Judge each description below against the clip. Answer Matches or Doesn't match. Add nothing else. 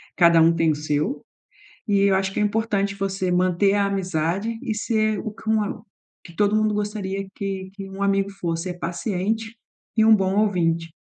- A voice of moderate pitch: Doesn't match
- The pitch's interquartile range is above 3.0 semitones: Doesn't match